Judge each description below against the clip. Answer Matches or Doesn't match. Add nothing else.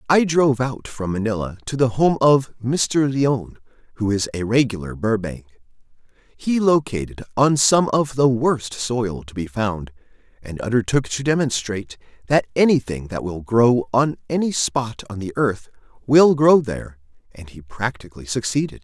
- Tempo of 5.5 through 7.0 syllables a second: Doesn't match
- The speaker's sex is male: Matches